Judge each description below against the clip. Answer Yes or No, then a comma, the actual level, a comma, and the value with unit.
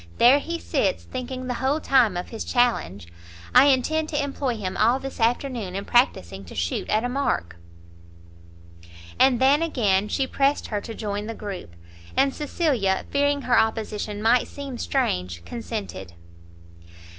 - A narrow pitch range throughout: No, average, 4.9 semitones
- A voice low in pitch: No, high, 240 Hz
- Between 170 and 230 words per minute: No, average, 155 wpm